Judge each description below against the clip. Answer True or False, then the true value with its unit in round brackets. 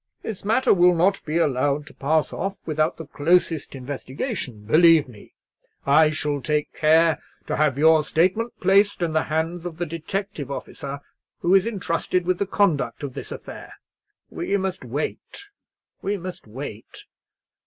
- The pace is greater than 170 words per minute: False (155 wpm)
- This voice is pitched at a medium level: True (160 Hz)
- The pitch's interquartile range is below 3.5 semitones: False (4.2 semitones)